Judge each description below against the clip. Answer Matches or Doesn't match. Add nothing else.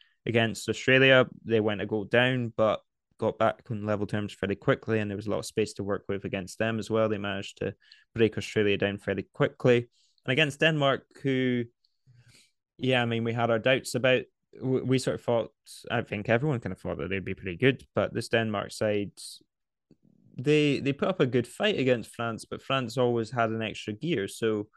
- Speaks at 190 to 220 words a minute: Matches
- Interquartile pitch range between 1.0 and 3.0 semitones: Doesn't match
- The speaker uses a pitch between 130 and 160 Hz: Doesn't match